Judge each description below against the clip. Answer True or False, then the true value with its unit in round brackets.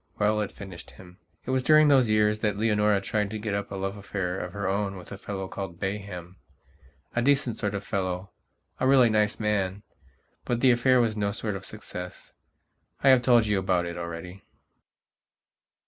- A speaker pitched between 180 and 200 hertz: False (100 Hz)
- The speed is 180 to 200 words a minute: True (185 wpm)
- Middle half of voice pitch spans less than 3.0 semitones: True (2.4 semitones)